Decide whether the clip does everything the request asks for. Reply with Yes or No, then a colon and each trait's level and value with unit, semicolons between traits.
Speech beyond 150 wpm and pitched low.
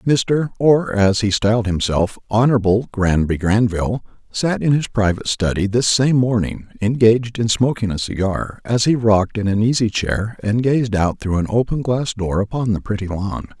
Yes: average, 170 wpm; low, 110 Hz